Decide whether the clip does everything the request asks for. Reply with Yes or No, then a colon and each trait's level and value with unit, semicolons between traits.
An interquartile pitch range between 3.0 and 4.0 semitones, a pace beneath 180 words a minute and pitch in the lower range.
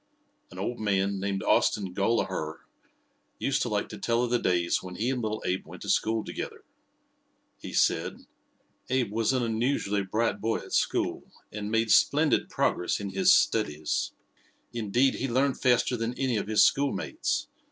Yes: average, 3.7 semitones; average, 165 wpm; low, 110 Hz